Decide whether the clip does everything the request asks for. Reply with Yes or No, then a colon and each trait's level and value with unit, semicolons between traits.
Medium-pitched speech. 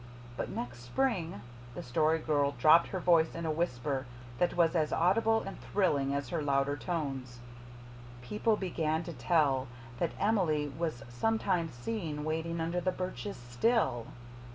Yes: medium, 160 Hz